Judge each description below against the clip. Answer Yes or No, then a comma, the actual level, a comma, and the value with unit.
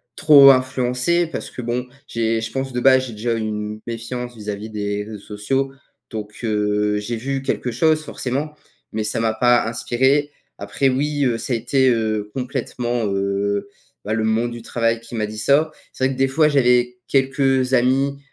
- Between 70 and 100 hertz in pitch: No, low, 120 Hz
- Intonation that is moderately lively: Yes, average, 3.5 semitones